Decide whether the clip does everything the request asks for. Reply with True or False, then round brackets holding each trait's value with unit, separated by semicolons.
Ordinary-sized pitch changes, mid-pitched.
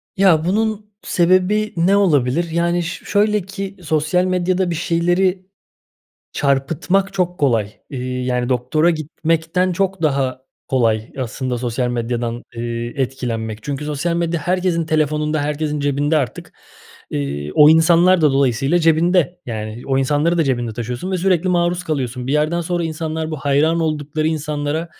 True (5.0 semitones; 155 Hz)